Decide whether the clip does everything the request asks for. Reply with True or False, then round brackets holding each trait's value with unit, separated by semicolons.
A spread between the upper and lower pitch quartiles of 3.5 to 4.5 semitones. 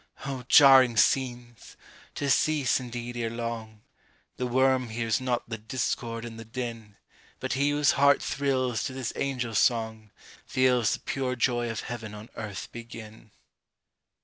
False (2.4 semitones)